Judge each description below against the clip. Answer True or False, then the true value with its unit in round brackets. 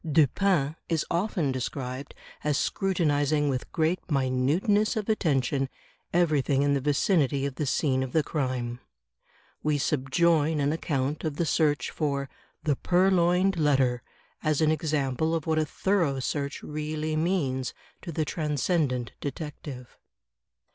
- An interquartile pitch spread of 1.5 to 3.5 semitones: True (3.2 semitones)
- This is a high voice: False (150 Hz)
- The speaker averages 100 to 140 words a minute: True (135 wpm)